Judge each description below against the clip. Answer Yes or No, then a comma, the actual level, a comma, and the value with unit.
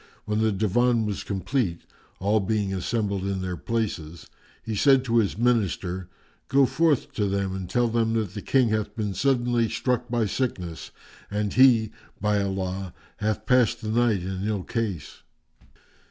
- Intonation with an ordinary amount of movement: Yes, average, 3.6 semitones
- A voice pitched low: Yes, low, 110 Hz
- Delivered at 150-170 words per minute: Yes, average, 160 wpm